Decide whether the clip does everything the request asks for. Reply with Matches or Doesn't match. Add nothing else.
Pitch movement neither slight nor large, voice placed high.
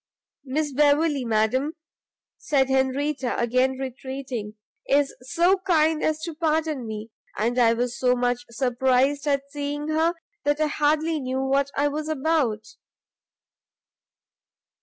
Matches